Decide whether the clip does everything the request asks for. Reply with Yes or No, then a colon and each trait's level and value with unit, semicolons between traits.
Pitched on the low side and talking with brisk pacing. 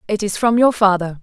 No: high, 205 Hz; fast, 245 wpm